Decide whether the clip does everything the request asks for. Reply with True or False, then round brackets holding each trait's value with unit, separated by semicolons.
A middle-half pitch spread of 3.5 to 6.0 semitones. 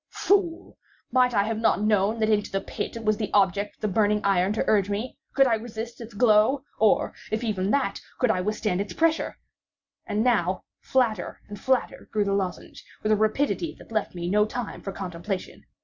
False (2.7 semitones)